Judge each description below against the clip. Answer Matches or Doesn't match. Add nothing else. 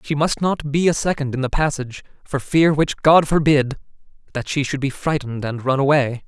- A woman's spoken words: Doesn't match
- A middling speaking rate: Matches